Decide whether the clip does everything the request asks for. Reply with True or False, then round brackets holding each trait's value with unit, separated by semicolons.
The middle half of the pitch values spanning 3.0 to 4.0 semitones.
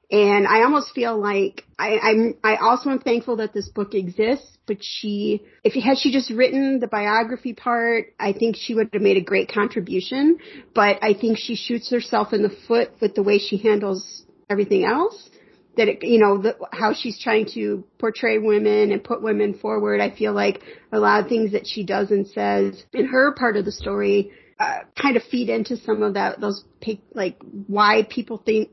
False (2.6 semitones)